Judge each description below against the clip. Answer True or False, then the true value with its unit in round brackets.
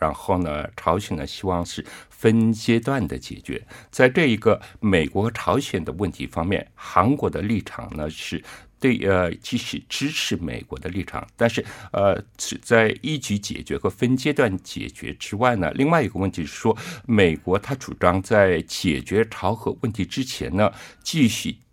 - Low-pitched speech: True (100 Hz)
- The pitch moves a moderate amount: True (4.7 semitones)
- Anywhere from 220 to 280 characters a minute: True (245 characters per minute)